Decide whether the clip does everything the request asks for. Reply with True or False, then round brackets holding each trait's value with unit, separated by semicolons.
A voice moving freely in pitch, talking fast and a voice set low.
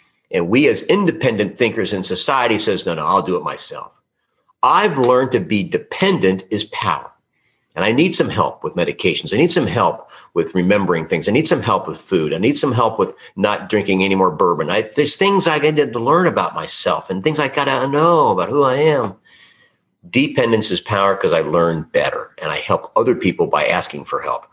True (7.8 semitones; 210 wpm; 130 Hz)